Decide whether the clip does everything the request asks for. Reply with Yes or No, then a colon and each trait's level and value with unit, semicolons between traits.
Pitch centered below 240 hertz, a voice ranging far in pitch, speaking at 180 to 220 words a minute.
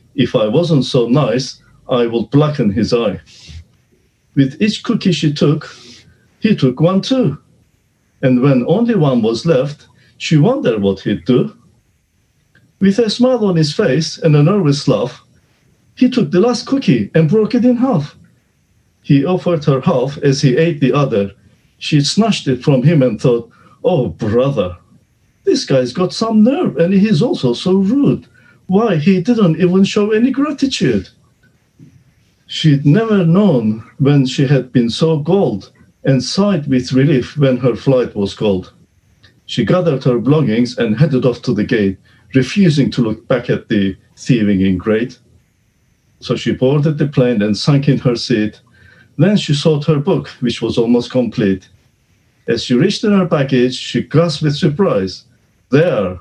No: medium, 140 Hz; wide, 6.6 semitones; average, 160 wpm